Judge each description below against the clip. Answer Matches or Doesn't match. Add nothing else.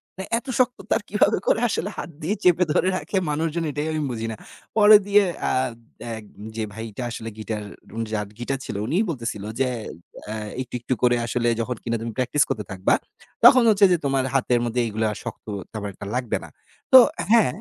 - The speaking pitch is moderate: Doesn't match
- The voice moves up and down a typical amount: Doesn't match